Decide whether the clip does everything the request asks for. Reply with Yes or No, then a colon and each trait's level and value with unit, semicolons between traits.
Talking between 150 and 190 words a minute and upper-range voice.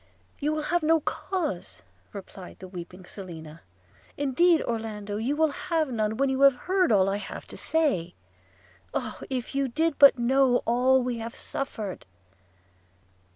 Yes: average, 155 wpm; high, 245 Hz